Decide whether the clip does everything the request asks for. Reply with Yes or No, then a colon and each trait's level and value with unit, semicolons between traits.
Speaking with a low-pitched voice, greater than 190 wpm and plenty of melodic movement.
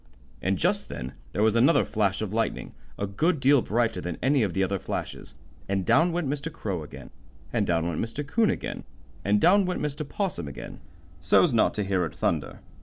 Yes: low, 110 Hz; average, 200 wpm; wide, 7.6 semitones